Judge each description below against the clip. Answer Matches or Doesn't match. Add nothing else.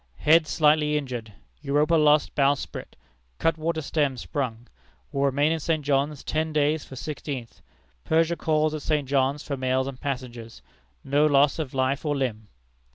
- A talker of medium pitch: Matches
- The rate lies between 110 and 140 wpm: Doesn't match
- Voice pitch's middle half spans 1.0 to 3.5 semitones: Matches